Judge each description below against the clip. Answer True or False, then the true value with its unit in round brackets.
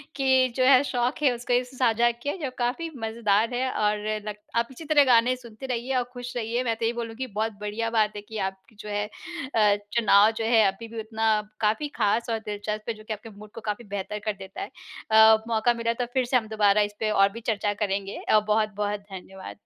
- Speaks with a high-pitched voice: True (225 Hz)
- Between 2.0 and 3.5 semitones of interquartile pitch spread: True (2.5 semitones)